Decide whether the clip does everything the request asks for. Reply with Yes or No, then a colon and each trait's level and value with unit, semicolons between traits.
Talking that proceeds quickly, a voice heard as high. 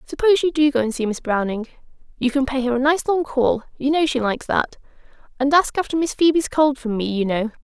Yes: fast, 245 wpm; very high, 270 Hz